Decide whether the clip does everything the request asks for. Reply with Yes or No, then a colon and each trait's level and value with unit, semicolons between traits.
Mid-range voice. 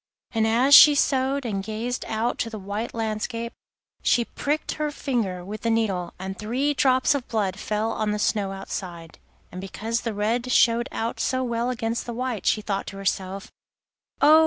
No: high, 225 Hz